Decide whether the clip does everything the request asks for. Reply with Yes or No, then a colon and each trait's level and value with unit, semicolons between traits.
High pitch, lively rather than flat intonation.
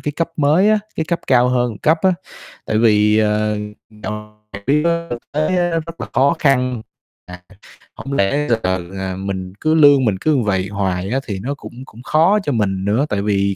No: low, 120 Hz; wide, 6.4 semitones